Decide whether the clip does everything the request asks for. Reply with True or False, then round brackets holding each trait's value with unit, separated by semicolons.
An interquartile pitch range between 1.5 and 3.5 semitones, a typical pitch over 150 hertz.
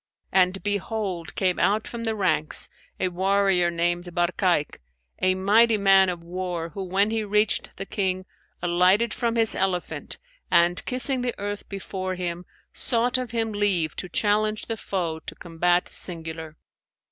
True (3.2 semitones; 190 Hz)